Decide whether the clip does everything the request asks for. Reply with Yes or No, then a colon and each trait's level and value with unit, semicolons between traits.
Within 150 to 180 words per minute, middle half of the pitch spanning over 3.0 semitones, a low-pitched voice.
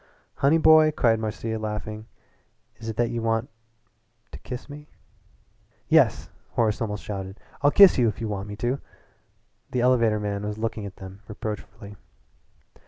No: average, 155 wpm; average, 2.7 semitones; low, 110 Hz